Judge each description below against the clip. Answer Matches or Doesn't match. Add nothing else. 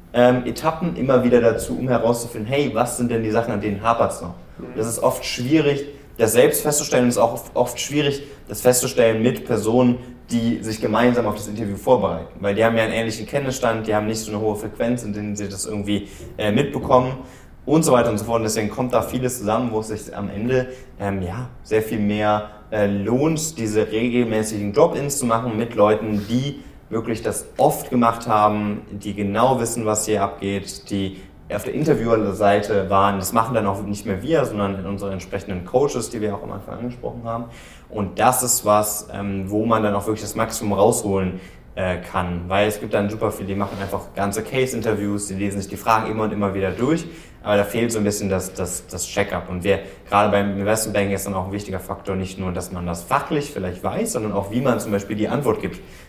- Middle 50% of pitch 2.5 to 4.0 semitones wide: Matches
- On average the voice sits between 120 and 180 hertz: Doesn't match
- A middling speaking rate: Doesn't match